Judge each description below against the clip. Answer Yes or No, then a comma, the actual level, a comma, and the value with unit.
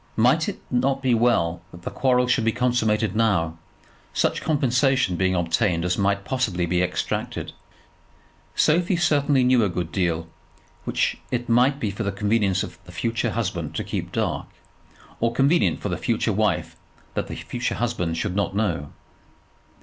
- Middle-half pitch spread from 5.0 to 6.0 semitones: Yes, wide, 5.6 semitones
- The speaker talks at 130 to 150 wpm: No, average, 165 wpm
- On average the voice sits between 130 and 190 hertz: No, low, 110 Hz